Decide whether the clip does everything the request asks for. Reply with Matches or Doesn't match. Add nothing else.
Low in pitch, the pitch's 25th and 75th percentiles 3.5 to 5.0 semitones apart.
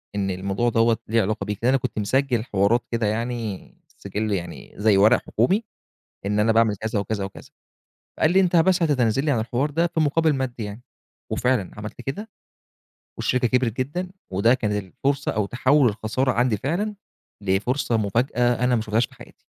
Matches